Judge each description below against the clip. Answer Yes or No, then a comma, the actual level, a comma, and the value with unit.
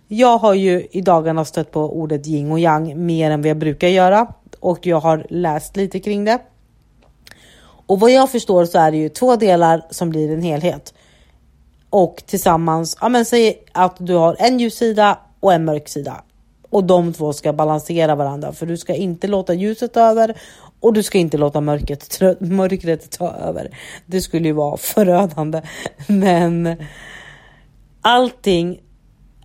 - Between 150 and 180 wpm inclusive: Yes, average, 165 wpm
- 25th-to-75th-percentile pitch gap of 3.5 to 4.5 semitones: Yes, average, 4.1 semitones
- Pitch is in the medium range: Yes, medium, 175 Hz